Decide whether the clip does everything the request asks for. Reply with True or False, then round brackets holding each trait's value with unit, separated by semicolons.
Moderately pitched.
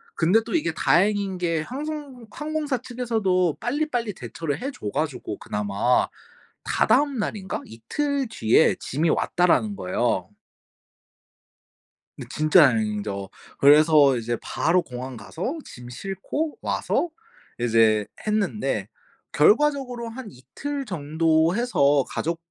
True (175 Hz)